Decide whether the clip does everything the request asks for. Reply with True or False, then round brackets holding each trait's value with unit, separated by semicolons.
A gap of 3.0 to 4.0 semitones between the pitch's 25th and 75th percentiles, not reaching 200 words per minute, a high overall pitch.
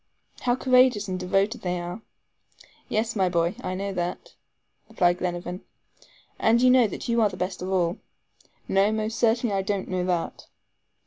True (3.7 semitones; 175 wpm; 195 Hz)